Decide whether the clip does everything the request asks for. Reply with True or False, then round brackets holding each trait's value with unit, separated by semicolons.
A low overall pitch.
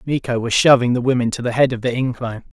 True (125 Hz)